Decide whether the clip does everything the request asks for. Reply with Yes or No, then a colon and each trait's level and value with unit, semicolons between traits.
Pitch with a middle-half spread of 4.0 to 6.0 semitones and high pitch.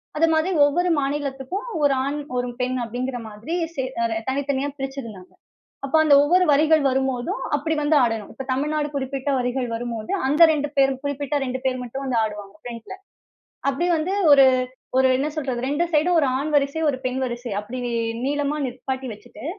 No: average, 2.8 semitones; very high, 270 Hz